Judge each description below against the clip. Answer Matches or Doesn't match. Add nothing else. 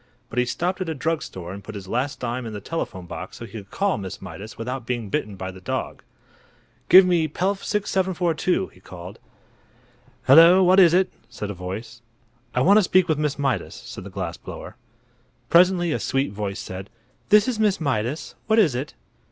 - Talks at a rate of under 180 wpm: Doesn't match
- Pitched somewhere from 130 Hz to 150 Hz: Matches